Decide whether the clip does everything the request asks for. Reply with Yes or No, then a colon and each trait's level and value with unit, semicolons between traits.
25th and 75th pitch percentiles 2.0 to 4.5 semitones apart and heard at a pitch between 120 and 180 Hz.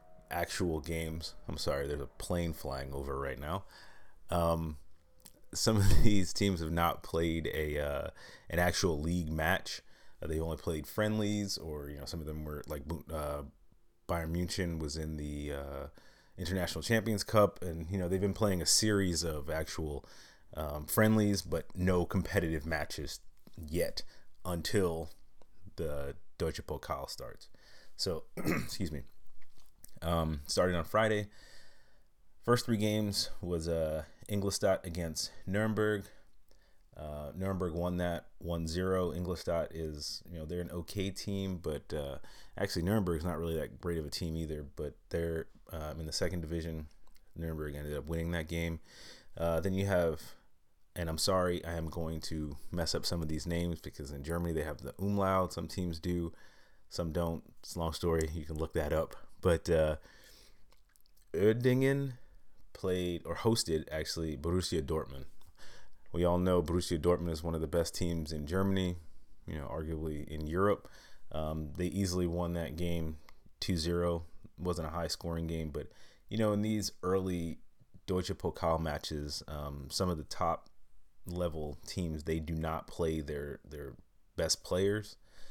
No: average, 2.9 semitones; very low, 85 Hz